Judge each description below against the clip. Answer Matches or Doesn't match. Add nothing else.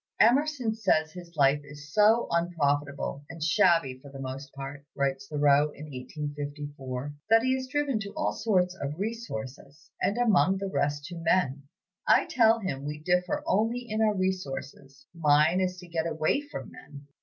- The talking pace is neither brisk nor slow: Matches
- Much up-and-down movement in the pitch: Matches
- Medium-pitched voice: Matches